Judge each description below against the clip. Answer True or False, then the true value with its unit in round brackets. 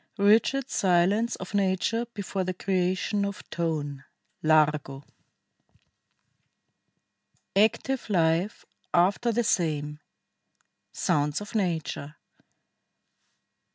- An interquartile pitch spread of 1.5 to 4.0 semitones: False (4.7 semitones)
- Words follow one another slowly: True (85 wpm)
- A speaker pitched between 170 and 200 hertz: True (185 Hz)